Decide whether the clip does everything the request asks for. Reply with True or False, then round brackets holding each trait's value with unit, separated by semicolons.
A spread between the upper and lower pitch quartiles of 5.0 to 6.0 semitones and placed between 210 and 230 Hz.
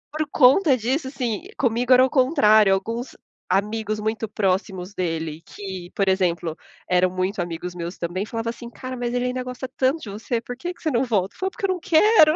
True (5.3 semitones; 225 Hz)